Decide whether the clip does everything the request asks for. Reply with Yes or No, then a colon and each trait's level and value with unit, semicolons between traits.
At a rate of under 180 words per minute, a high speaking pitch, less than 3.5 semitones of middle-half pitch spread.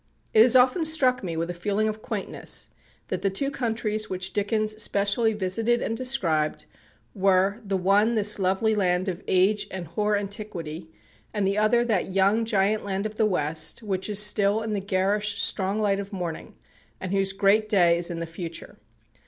No: average, 185 wpm; high, 200 Hz; narrow, 2.4 semitones